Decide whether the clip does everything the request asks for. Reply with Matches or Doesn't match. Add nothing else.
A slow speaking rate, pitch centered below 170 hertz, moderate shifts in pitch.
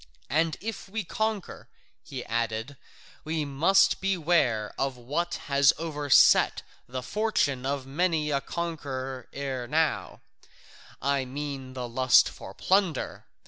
Matches